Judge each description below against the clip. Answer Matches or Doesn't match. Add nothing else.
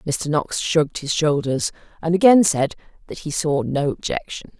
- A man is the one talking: Doesn't match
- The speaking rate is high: Doesn't match